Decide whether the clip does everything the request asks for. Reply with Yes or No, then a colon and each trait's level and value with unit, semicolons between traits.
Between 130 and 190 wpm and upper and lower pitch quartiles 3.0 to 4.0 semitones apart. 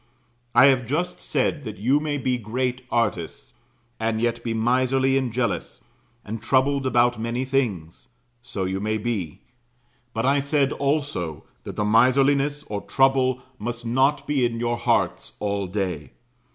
Yes: average, 150 wpm; average, 3.6 semitones